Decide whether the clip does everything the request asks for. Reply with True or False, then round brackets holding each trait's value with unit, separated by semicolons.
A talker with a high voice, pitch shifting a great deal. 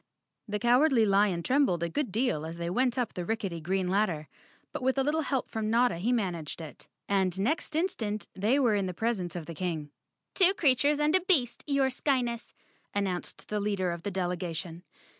True (210 Hz; 6.4 semitones)